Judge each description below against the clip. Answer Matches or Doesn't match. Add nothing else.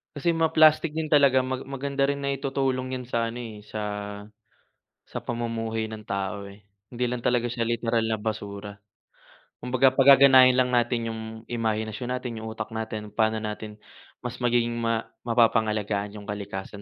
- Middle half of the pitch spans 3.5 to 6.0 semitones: Doesn't match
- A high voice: Doesn't match